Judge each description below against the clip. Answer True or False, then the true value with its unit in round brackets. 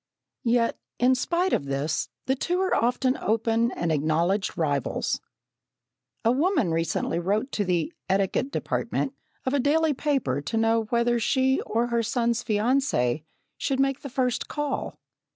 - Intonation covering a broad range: True (5.9 semitones)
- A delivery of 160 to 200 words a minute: False (150 wpm)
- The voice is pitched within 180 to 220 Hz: False (235 Hz)